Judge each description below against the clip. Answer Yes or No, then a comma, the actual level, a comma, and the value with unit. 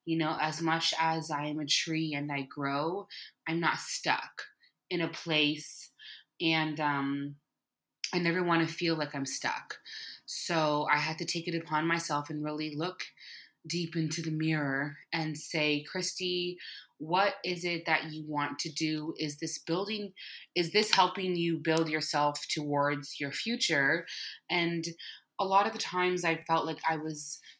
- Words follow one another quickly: No, average, 165 wpm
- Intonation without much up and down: Yes, narrow, 2.1 semitones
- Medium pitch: Yes, medium, 160 Hz